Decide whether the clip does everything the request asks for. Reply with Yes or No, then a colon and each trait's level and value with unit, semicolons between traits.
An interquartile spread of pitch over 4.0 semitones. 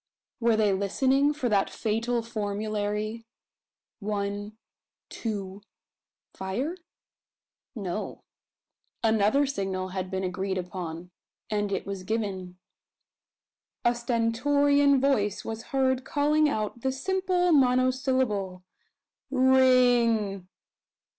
Yes: average, 4.7 semitones